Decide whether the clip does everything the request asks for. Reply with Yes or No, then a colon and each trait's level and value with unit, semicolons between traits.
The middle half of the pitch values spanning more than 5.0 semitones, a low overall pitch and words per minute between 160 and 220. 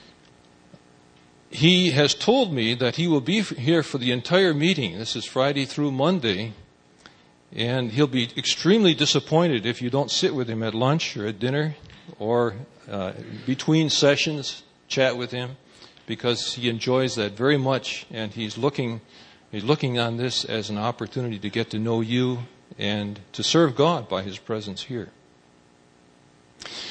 Yes: wide, 5.5 semitones; low, 120 Hz; average, 165 wpm